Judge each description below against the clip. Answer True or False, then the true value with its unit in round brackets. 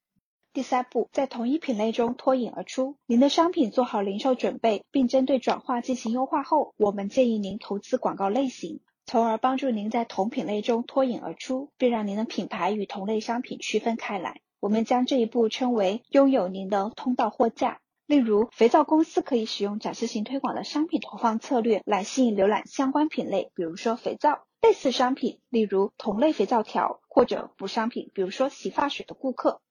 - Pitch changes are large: False (3.9 semitones)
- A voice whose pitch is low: False (240 Hz)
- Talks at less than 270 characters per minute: False (305 characters per minute)